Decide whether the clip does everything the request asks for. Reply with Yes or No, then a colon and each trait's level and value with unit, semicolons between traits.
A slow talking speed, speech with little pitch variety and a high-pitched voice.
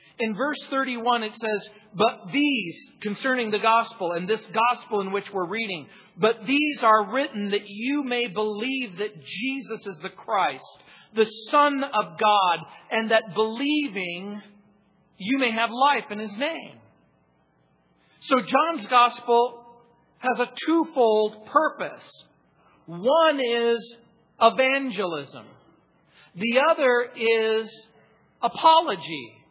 No: slow, 120 wpm; average, 3.8 semitones; high, 225 Hz